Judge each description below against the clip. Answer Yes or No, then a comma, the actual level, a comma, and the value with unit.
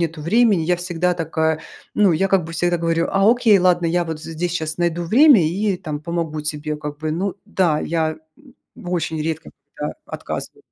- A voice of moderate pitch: Yes, medium, 170 Hz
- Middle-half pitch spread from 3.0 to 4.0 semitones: No, narrow, 2.5 semitones